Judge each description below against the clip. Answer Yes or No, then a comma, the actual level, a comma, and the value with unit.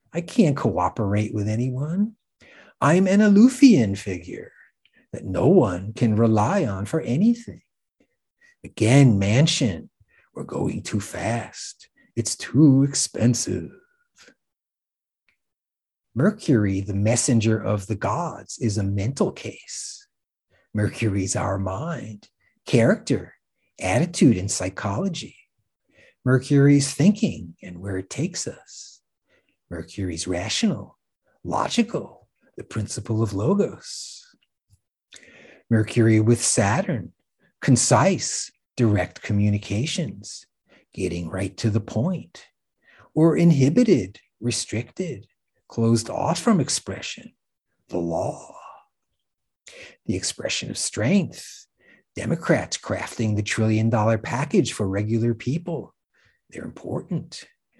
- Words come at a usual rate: No, slow, 95 wpm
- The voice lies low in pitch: Yes, low, 115 Hz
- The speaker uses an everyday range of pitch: No, wide, 7.4 semitones